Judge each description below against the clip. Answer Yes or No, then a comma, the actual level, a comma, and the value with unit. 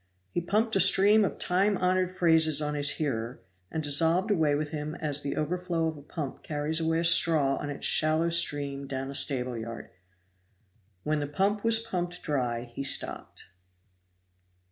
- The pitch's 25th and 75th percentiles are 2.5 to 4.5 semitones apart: Yes, average, 3.8 semitones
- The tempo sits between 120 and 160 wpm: No, average, 170 wpm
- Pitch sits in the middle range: Yes, medium, 155 Hz